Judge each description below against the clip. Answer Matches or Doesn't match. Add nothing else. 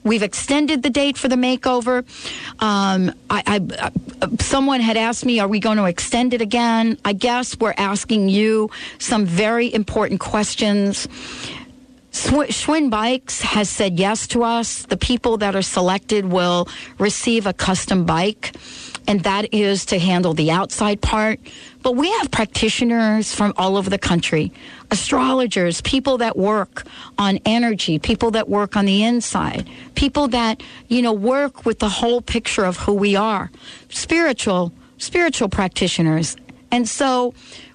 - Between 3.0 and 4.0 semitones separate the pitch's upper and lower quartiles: Matches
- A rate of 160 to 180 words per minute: Doesn't match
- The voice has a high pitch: Matches